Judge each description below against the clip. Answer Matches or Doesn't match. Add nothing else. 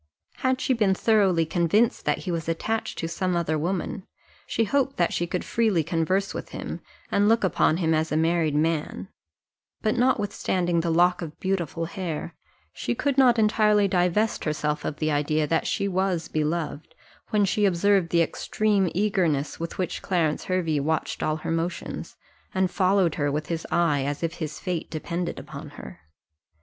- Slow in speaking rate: Doesn't match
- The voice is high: Doesn't match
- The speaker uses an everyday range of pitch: Matches